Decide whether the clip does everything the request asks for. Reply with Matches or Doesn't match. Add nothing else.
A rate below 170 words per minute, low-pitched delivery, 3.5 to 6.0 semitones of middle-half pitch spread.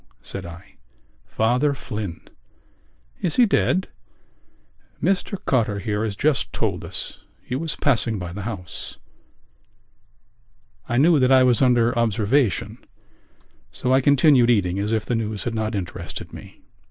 Matches